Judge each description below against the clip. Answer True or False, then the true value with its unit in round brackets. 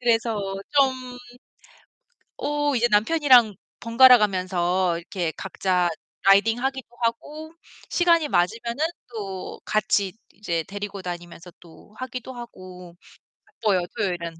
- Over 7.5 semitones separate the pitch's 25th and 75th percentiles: False (5.5 semitones)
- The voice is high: True (215 Hz)